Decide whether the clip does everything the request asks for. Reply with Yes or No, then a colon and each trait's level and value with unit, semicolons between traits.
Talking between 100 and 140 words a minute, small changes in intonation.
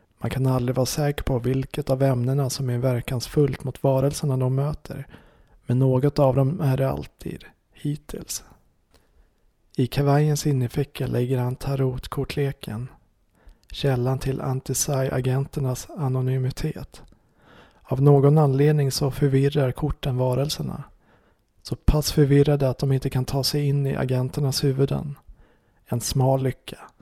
Yes: average, 130 wpm; narrow, 1.7 semitones